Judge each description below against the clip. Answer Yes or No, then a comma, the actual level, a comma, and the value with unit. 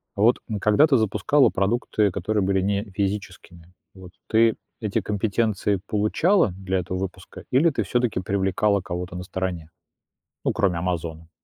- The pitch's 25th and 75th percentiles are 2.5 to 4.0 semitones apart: Yes, average, 2.8 semitones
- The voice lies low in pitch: Yes, low, 100 Hz